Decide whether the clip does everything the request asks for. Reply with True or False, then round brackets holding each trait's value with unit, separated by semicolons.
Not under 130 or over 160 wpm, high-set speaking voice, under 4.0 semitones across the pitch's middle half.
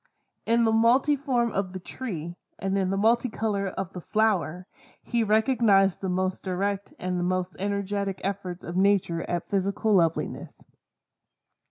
True (145 wpm; 195 Hz; 3.1 semitones)